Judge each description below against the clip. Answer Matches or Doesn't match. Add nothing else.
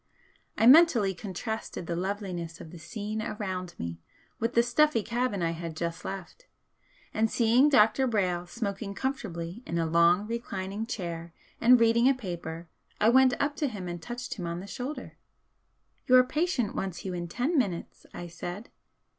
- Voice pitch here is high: Matches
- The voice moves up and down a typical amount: Doesn't match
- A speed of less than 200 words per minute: Matches